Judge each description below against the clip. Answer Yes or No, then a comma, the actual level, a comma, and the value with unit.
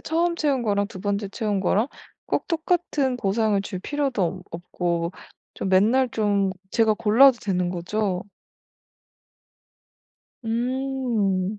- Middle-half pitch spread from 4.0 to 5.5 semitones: Yes, average, 5.2 semitones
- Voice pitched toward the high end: Yes, high, 210 Hz